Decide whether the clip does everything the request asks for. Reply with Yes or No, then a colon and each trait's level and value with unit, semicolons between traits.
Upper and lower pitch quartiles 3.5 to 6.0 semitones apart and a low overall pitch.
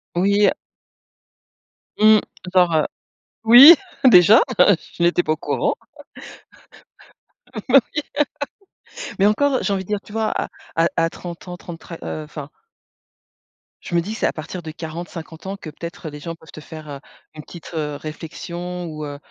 No: average, 4.2 semitones; medium, 170 Hz